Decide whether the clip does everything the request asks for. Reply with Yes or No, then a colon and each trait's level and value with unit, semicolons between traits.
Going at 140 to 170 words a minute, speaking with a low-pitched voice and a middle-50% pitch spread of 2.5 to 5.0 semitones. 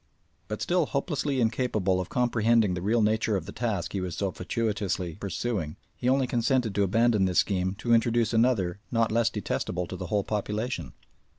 No: average, 180 wpm; low, 110 Hz; average, 3.7 semitones